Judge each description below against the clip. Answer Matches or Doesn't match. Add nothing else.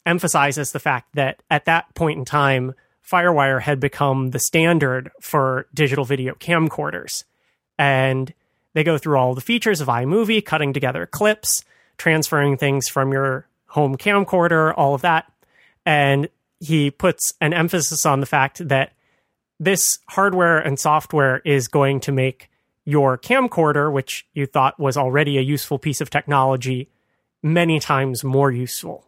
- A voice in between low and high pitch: Matches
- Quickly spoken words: Doesn't match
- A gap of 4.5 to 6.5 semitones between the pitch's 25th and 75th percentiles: Doesn't match